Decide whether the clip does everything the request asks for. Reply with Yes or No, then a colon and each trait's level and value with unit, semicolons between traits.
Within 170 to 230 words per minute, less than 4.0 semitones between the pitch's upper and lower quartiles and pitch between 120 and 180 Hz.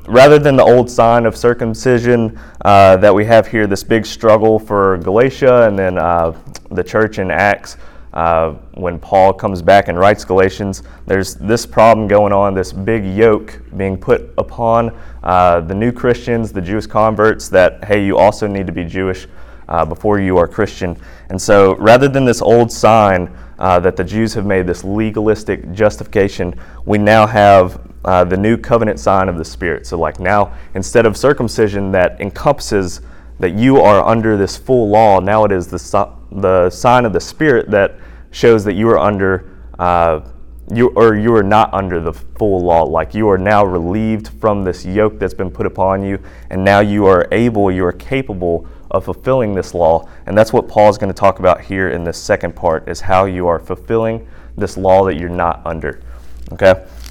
No: average, 190 wpm; average, 3.3 semitones; low, 100 Hz